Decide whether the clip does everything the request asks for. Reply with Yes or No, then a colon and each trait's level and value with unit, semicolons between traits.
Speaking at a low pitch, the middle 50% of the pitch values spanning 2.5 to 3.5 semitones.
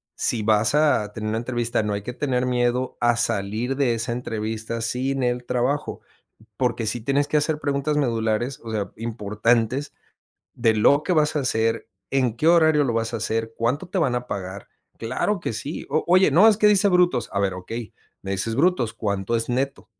No: low, 120 Hz; average, 4.0 semitones